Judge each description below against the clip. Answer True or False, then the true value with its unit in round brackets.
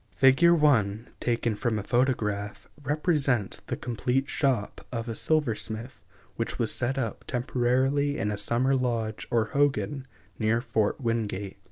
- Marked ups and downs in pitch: False (3.6 semitones)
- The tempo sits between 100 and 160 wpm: True (140 wpm)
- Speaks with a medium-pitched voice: False (120 Hz)